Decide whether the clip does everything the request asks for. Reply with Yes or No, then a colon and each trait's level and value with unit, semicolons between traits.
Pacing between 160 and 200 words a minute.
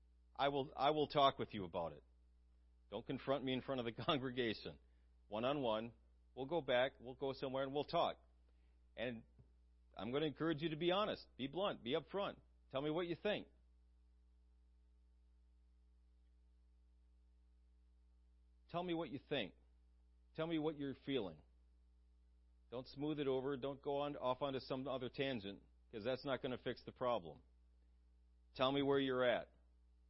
Yes: average, 165 wpm